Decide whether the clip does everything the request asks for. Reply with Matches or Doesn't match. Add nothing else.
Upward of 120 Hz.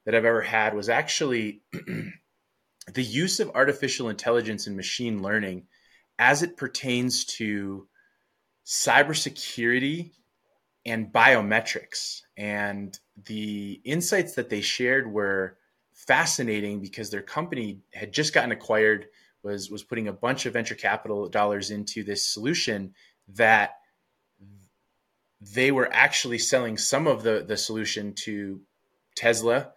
Doesn't match